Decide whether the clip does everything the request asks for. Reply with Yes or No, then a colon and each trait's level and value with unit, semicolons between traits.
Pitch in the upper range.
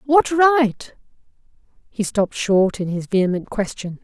Yes: high, 225 Hz